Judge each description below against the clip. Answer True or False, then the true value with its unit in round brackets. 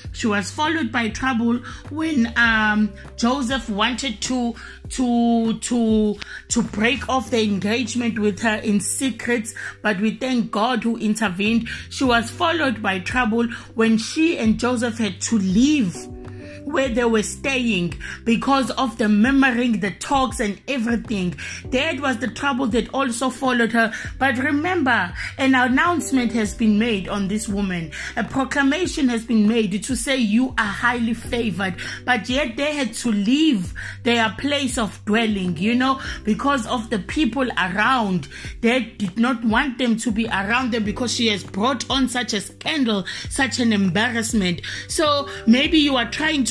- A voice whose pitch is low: False (235 Hz)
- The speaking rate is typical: True (160 wpm)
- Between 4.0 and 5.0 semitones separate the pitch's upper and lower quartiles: False (3.3 semitones)